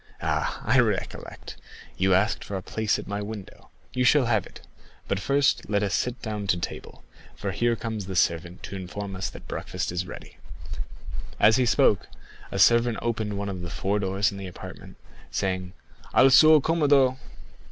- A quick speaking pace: No, average, 180 wpm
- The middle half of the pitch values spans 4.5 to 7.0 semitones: No, average, 3.8 semitones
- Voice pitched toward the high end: No, low, 100 Hz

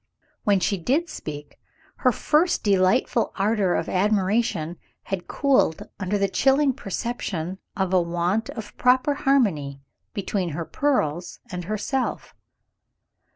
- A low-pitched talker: No, high, 200 Hz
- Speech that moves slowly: Yes, slow, 120 wpm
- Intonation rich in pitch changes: Yes, wide, 5.9 semitones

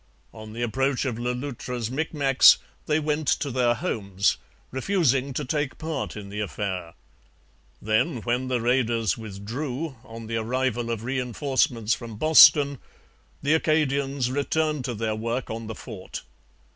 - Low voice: Yes, low, 125 Hz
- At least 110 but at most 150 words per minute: Yes, average, 145 wpm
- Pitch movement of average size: Yes, average, 3.9 semitones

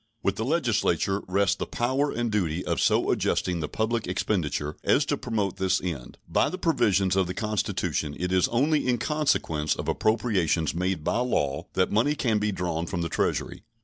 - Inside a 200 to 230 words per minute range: No, average, 185 wpm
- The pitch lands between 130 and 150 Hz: No, low, 100 Hz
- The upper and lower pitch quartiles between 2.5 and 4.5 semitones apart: No, average, 5.2 semitones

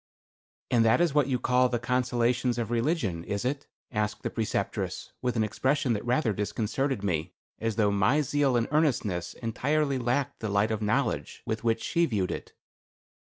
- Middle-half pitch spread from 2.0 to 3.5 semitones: No, average, 3.9 semitones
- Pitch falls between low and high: No, low, 120 Hz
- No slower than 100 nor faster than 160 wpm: No, average, 175 wpm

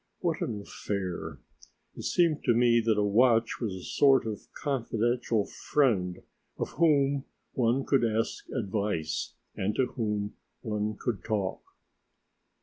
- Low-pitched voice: Yes, low, 115 Hz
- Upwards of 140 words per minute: No, slow, 135 wpm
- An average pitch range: Yes, average, 3.9 semitones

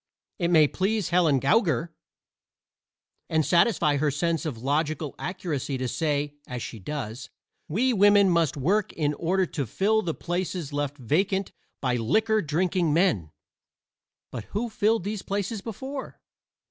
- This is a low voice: No, medium, 165 Hz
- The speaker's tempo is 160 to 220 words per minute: No, average, 140 wpm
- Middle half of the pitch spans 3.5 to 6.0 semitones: Yes, average, 5.2 semitones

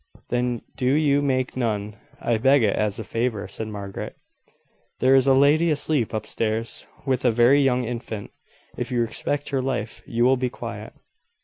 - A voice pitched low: Yes, low, 125 Hz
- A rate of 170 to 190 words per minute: Yes, average, 180 wpm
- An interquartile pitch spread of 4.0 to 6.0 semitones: No, average, 3.2 semitones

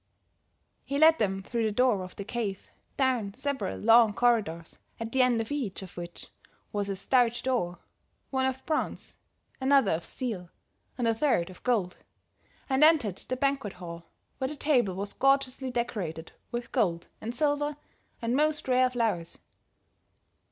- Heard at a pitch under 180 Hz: No, high, 235 Hz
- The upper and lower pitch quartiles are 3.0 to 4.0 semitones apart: No, average, 5.1 semitones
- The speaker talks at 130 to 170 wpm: Yes, average, 160 wpm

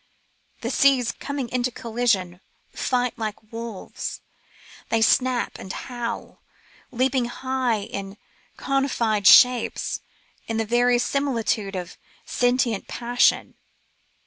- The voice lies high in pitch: Yes, high, 240 Hz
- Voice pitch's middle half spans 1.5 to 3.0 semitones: Yes, narrow, 2.4 semitones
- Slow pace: Yes, slow, 100 wpm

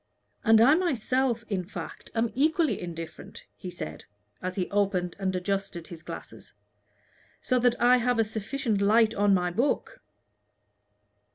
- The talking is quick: No, average, 145 wpm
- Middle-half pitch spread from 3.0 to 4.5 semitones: No, average, 5.0 semitones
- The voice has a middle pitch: No, high, 215 Hz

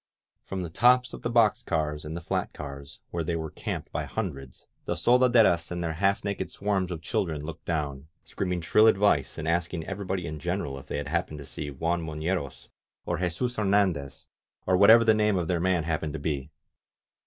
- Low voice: Yes, very low, 85 Hz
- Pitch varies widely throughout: No, average, 4.4 semitones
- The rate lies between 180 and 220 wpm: Yes, fast, 205 wpm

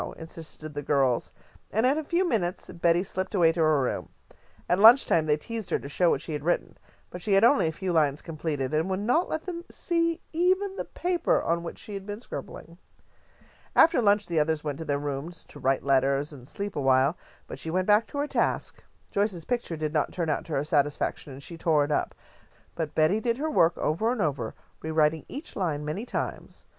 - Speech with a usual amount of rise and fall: No, wide, 6.1 semitones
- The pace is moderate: No, fast, 220 wpm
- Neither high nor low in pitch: Yes, medium, 165 Hz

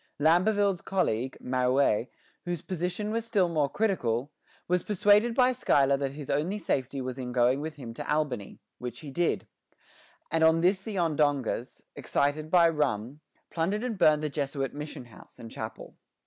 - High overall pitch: No, medium, 150 Hz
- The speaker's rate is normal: Yes, average, 160 wpm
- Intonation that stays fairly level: No, wide, 5.4 semitones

